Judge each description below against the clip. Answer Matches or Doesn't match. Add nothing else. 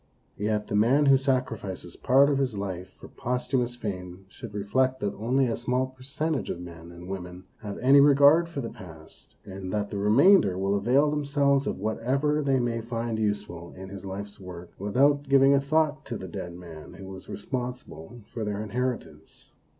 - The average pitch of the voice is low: Matches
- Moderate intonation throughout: Doesn't match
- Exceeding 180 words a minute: Matches